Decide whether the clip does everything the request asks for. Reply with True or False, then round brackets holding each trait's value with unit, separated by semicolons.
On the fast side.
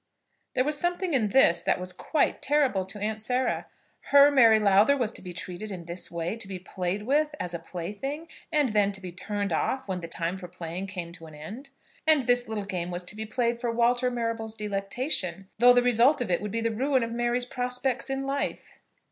True (220 wpm)